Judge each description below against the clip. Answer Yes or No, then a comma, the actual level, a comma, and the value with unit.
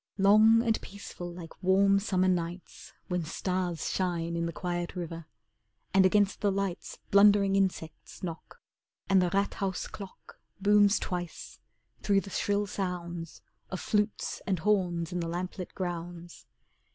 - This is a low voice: No, medium, 185 Hz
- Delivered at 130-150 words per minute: Yes, average, 140 wpm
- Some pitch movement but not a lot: No, narrow, 2.3 semitones